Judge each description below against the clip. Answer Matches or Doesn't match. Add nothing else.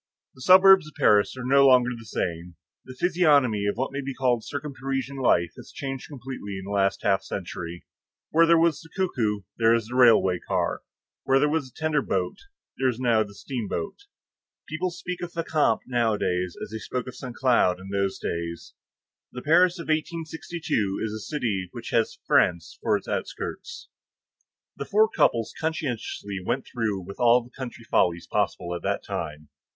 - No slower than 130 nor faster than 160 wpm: Doesn't match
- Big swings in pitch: Matches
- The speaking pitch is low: Matches